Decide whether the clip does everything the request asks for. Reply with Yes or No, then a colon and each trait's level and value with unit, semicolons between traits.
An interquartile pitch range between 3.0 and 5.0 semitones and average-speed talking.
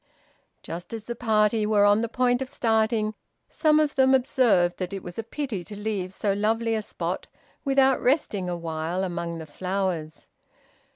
Yes: average, 4.7 semitones; average, 170 wpm